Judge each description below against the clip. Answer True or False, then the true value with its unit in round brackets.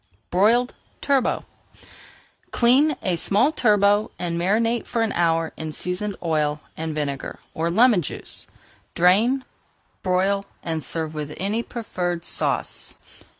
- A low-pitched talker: False (185 Hz)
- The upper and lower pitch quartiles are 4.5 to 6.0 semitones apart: True (5.6 semitones)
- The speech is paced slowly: True (120 wpm)